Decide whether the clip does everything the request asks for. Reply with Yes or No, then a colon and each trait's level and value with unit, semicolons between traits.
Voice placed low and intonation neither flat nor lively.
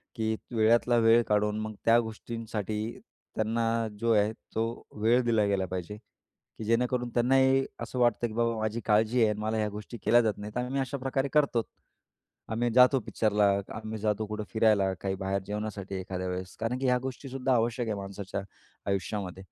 No: low, 110 Hz; narrow, 2.3 semitones